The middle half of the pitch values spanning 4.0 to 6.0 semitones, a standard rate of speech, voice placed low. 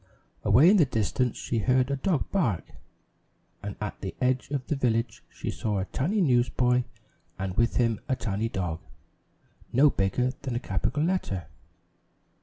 Yes: average, 4.6 semitones; average, 160 wpm; low, 125 Hz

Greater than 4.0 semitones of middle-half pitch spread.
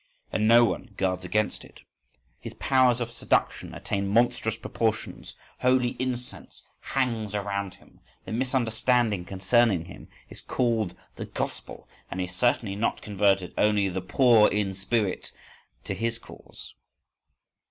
No: average, 3.5 semitones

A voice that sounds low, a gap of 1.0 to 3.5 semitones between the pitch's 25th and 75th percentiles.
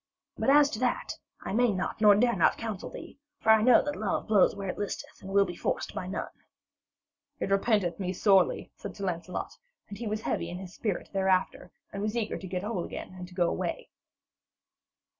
No: high, 200 Hz; average, 3.0 semitones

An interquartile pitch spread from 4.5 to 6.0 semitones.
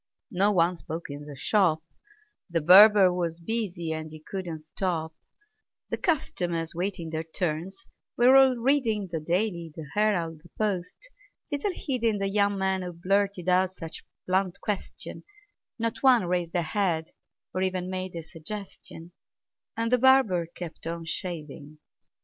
No: average, 3.9 semitones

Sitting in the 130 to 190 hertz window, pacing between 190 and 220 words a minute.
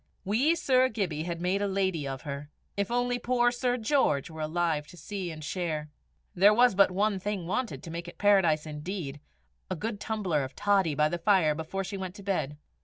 Yes: medium, 185 Hz; fast, 205 wpm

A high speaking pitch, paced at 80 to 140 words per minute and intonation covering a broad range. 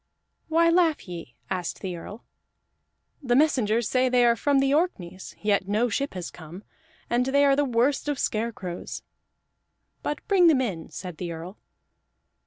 No: high, 235 Hz; average, 160 wpm; wide, 7.3 semitones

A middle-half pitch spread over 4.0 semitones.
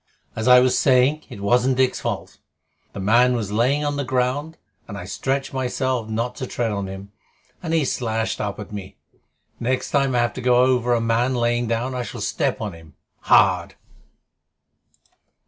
No: narrow, 2.6 semitones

